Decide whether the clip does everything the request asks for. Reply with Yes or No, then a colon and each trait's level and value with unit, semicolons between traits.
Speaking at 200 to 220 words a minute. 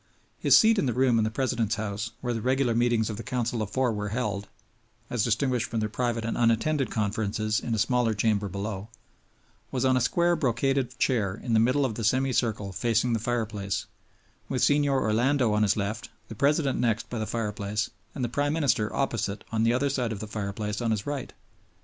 Yes: fast, 205 wpm